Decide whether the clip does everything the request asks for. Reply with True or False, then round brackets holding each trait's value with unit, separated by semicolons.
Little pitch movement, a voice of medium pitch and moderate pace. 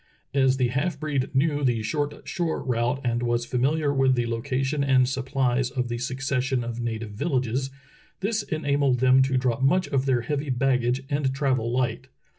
False (2.3 semitones; 130 Hz; 175 wpm)